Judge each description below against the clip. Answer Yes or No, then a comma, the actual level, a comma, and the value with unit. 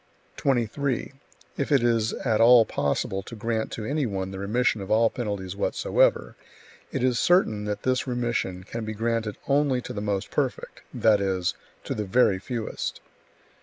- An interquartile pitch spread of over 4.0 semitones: No, average, 3.4 semitones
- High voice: No, low, 115 Hz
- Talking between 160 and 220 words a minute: Yes, average, 165 wpm